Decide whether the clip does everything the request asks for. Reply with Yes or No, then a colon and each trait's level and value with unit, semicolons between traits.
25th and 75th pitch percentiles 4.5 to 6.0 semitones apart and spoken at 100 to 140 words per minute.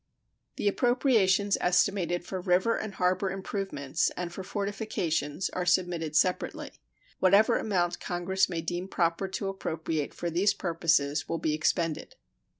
No: average, 2.7 semitones; slow, 135 wpm